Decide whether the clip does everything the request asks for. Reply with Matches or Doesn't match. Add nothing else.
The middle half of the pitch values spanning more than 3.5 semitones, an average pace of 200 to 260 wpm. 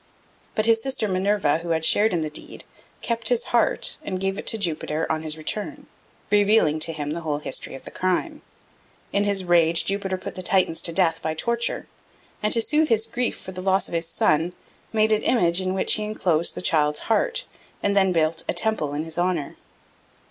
Matches